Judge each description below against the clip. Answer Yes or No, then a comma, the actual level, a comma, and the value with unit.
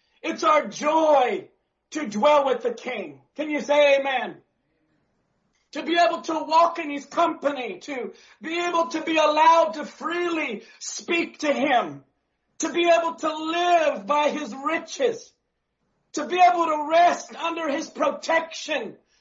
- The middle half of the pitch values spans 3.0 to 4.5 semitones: No, narrow, 2.4 semitones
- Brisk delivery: No, average, 145 wpm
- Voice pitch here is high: Yes, very high, 315 Hz